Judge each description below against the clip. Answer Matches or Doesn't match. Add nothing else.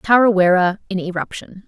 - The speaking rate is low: Matches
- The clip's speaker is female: Matches